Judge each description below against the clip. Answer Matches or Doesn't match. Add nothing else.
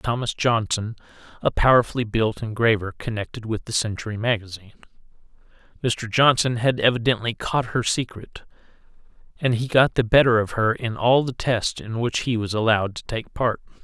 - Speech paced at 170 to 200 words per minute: Doesn't match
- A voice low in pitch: Matches